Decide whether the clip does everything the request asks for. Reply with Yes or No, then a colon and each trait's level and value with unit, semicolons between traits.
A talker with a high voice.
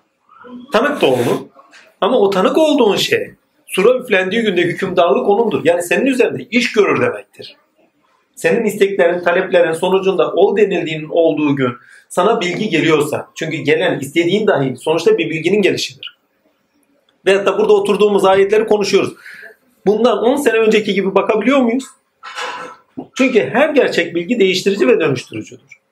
Yes: high, 200 Hz